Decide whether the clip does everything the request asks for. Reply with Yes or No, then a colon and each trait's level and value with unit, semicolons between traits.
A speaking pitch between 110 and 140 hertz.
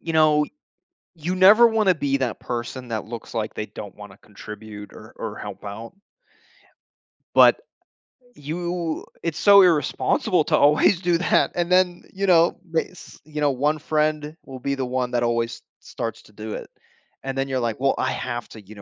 Yes: low, 135 Hz